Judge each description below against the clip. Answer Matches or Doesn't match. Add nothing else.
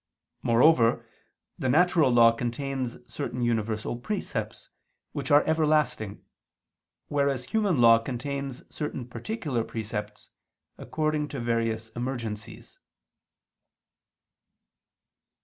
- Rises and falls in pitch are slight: Doesn't match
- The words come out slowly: Matches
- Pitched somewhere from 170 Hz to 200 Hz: Doesn't match